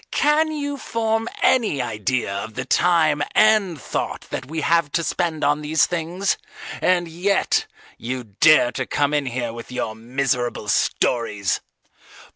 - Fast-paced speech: No, average, 145 wpm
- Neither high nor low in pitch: Yes, medium, 150 Hz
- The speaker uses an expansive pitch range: Yes, wide, 6.7 semitones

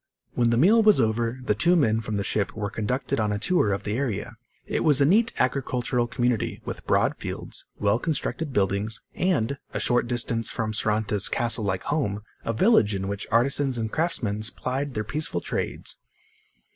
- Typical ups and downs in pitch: Yes, average, 4.5 semitones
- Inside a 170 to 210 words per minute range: Yes, average, 185 wpm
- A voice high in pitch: No, low, 120 Hz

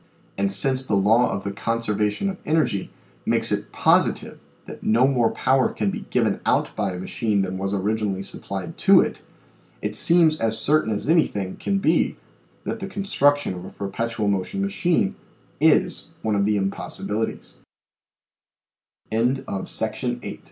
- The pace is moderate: Yes, average, 150 wpm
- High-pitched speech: No, low, 110 Hz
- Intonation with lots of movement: Yes, wide, 5.7 semitones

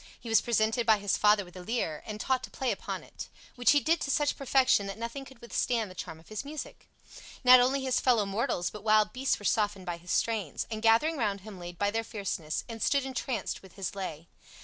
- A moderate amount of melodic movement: Yes, average, 4.2 semitones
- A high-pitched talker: Yes, high, 220 Hz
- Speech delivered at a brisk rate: Yes, fast, 235 wpm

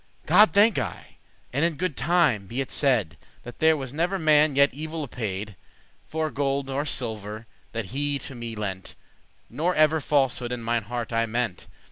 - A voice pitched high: No, low, 135 Hz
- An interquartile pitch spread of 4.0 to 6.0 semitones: Yes, average, 5.1 semitones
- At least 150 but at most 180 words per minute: No, average, 190 wpm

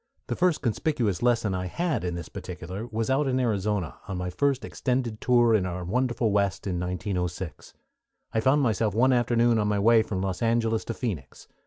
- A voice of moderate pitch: No, low, 110 Hz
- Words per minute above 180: Yes, average, 190 wpm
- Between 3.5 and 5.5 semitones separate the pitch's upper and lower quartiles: Yes, average, 4.6 semitones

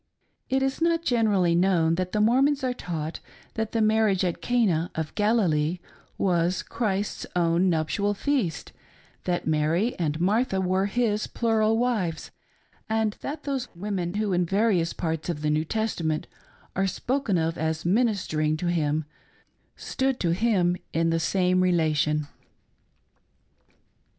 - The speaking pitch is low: No, medium, 185 Hz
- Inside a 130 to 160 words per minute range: Yes, average, 140 wpm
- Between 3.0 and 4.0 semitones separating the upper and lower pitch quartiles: No, average, 5.1 semitones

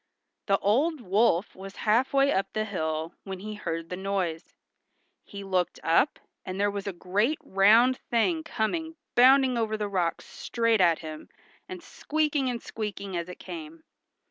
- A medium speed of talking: Yes, average, 165 wpm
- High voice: Yes, high, 205 Hz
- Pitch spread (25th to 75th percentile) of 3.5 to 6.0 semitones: Yes, average, 5.0 semitones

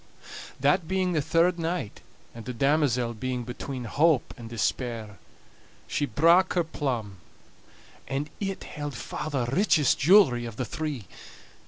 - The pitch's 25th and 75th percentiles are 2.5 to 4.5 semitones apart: No, wide, 5.4 semitones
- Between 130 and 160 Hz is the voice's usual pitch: Yes, medium, 140 Hz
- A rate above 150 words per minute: No, average, 140 wpm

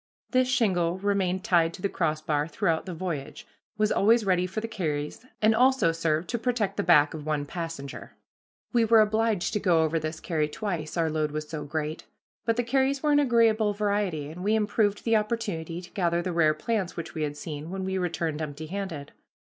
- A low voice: No, medium, 180 Hz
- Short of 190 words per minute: No, average, 200 wpm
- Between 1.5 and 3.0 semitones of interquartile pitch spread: No, average, 5.3 semitones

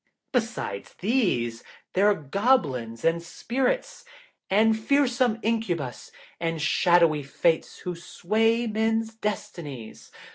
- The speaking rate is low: Yes, slow, 100 wpm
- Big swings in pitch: Yes, wide, 5.8 semitones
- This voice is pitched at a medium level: No, high, 200 Hz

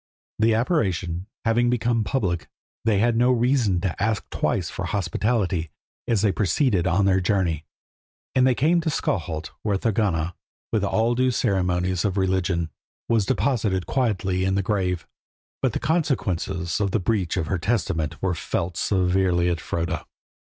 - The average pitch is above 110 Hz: No, very low, 95 Hz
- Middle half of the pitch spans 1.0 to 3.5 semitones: No, average, 4.2 semitones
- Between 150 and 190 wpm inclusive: Yes, average, 155 wpm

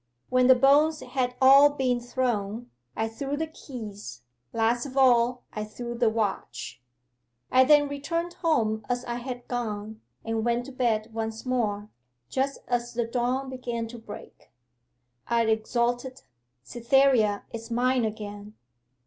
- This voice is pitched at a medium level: No, high, 240 Hz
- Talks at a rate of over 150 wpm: No, average, 140 wpm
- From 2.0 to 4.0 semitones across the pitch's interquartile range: Yes, average, 2.8 semitones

